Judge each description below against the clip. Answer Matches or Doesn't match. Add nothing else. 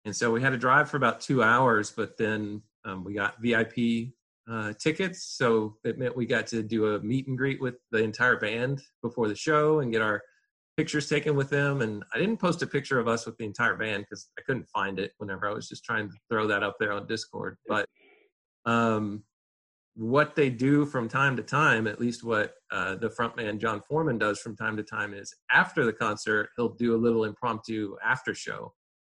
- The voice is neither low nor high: Doesn't match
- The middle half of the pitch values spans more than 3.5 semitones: Matches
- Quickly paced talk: Matches